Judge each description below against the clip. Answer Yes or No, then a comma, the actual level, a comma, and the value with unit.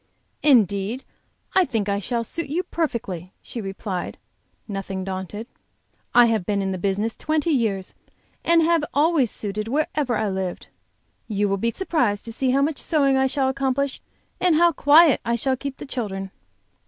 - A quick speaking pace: No, average, 165 wpm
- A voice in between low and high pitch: No, high, 235 Hz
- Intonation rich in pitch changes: Yes, wide, 6.2 semitones